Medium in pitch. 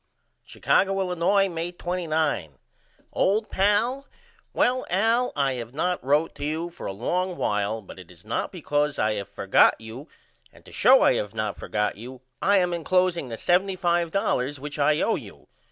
Yes: medium, 165 Hz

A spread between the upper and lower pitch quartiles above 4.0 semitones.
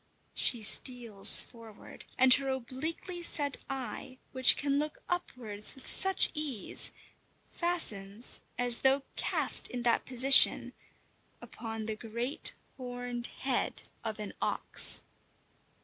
No: average, 3.1 semitones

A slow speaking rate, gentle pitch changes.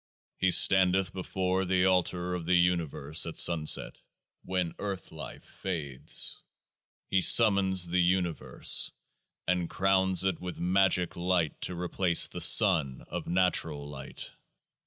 Yes: slow, 125 wpm; narrow, 1.7 semitones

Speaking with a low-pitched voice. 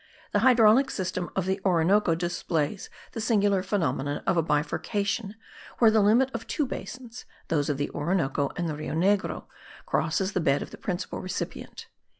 No: high, 190 Hz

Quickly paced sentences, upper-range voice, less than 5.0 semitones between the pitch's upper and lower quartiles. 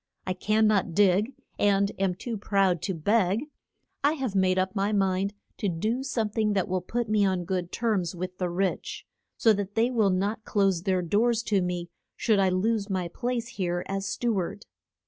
No: average, 195 wpm; high, 195 Hz; average, 2.9 semitones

